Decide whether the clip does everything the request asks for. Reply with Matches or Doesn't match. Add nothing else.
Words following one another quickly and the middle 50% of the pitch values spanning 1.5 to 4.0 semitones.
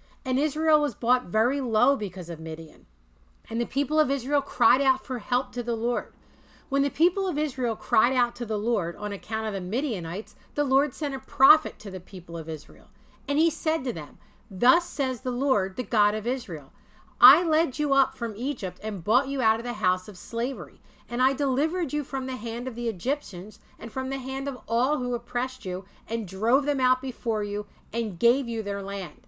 Doesn't match